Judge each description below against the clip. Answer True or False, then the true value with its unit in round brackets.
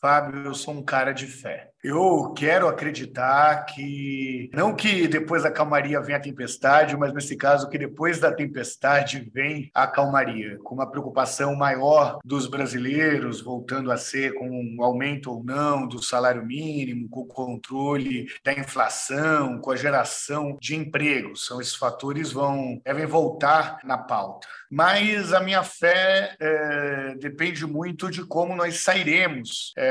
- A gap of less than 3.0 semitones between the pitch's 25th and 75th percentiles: True (2.6 semitones)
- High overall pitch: False (140 Hz)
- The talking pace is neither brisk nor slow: True (155 wpm)